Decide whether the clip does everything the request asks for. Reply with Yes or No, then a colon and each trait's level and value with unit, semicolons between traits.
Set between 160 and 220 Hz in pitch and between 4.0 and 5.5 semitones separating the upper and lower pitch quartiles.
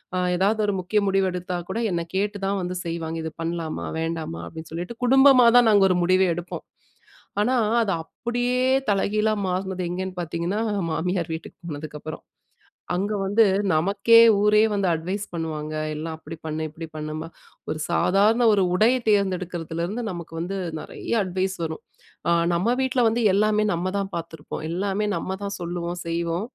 No: medium, 185 Hz; average, 3.6 semitones